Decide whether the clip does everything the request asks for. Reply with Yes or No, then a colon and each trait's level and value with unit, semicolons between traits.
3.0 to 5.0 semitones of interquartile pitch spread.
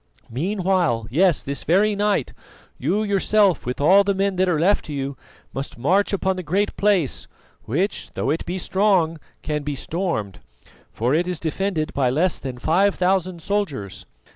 No: wide, 5.4 semitones